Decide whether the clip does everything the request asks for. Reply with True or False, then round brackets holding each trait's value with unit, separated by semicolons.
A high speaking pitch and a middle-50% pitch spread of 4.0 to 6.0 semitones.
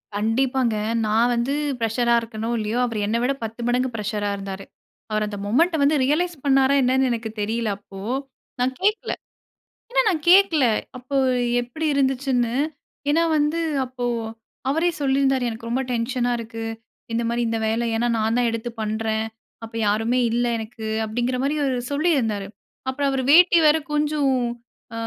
False (245 Hz; 3.6 semitones)